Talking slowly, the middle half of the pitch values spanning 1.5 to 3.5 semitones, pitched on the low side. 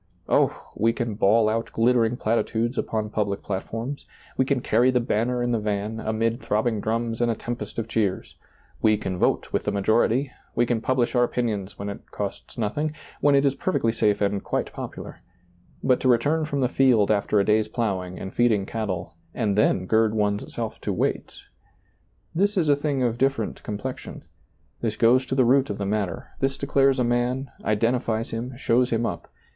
No: average, 195 wpm; average, 3.1 semitones; low, 115 Hz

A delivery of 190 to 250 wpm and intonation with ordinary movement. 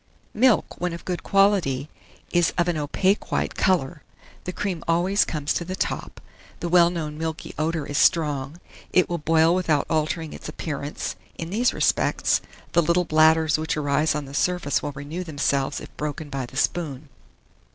No: average, 170 wpm; average, 3.0 semitones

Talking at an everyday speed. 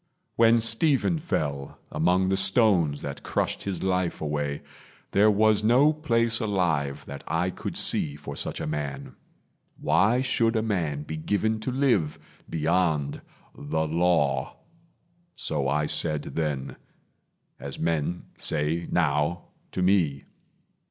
No: slow, 130 wpm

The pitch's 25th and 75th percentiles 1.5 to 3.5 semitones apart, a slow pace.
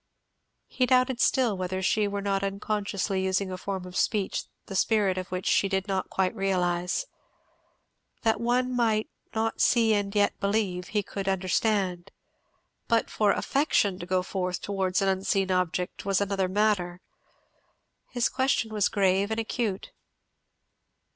No: narrow, 2.6 semitones; average, 145 wpm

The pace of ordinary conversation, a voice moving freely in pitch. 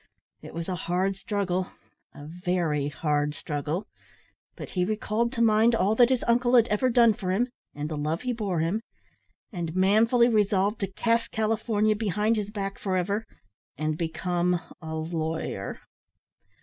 No: average, 160 wpm; average, 4.8 semitones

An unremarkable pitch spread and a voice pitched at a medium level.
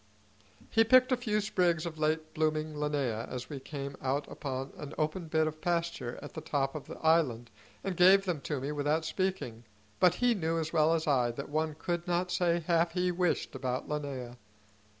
Yes: average, 3.7 semitones; medium, 155 Hz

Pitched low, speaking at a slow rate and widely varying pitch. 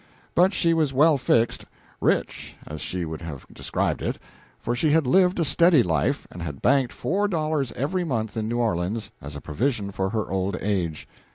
No: low, 120 Hz; average, 190 wpm; wide, 8.9 semitones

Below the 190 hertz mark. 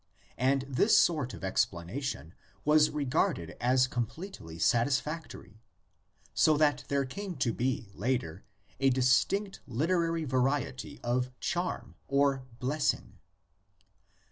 Yes: low, 135 Hz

